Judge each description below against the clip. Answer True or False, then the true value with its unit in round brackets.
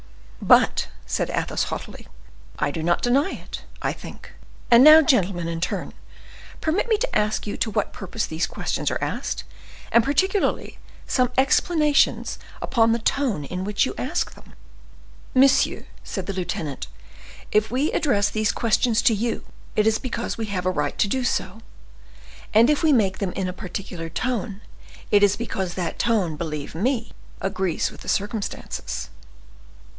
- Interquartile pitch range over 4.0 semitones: True (5.2 semitones)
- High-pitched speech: True (215 Hz)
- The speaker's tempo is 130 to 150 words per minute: False (160 wpm)